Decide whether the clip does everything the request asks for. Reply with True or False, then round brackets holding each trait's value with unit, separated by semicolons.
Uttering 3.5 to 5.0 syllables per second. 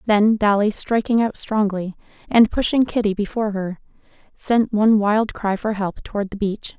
True (4.9 syllables/s)